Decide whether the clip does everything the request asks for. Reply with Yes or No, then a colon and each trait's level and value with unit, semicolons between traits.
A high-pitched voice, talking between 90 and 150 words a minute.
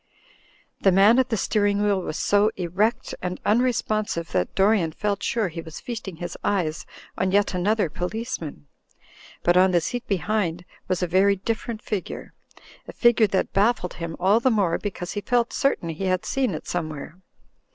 No: high, 195 Hz; average, 175 wpm